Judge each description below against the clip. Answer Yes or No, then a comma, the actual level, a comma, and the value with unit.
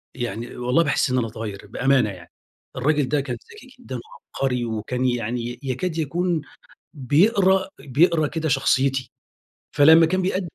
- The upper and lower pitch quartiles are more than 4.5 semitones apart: Yes, average, 5.1 semitones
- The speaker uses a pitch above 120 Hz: Yes, low, 135 Hz